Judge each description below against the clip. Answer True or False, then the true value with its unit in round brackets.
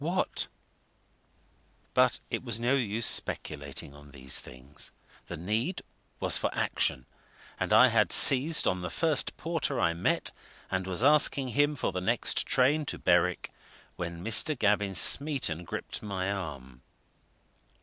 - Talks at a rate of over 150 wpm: False (140 wpm)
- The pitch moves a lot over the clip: True (7.5 semitones)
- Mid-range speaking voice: False (105 Hz)